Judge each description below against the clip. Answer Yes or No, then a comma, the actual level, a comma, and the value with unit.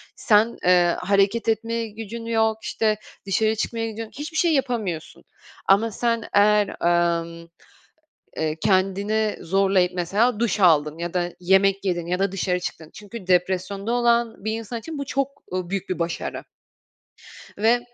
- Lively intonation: No, average, 3.9 semitones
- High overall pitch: Yes, high, 200 Hz